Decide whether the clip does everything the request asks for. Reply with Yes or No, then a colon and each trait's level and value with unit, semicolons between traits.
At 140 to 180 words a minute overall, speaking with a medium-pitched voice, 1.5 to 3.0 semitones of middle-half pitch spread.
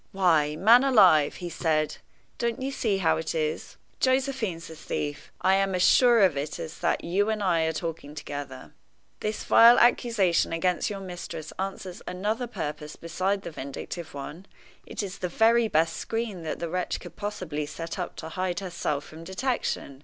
No: average, 175 wpm; medium, 180 Hz; average, 4.8 semitones